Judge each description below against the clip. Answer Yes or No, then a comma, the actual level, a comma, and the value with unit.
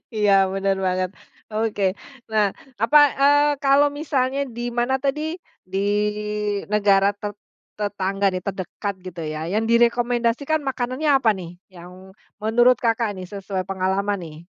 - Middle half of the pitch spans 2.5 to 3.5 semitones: No, average, 4.6 semitones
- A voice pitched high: Yes, high, 215 Hz